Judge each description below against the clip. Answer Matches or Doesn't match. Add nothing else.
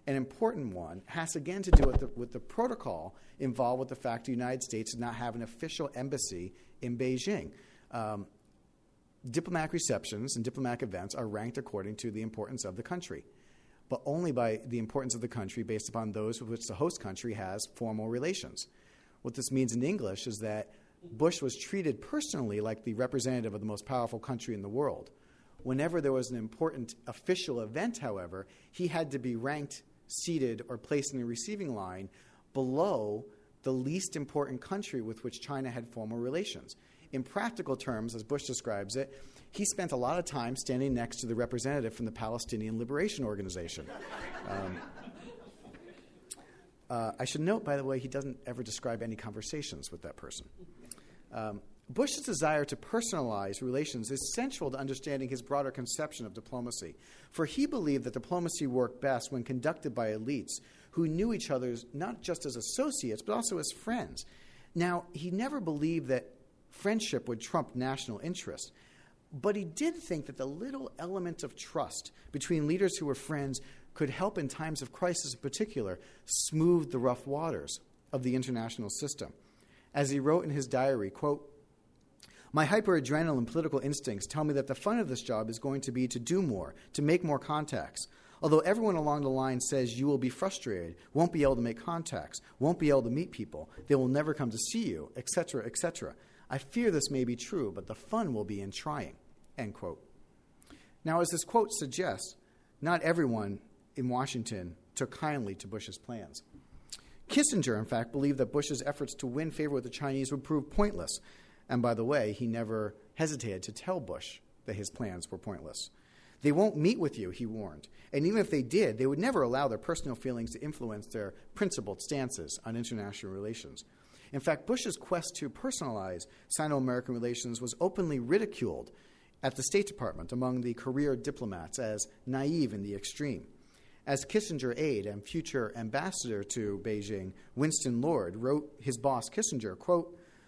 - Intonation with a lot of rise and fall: Doesn't match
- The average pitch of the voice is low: Matches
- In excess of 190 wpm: Doesn't match